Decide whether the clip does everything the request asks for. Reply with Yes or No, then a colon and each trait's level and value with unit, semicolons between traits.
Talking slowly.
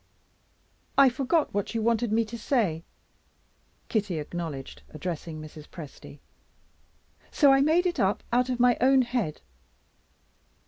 Yes: slow, 130 wpm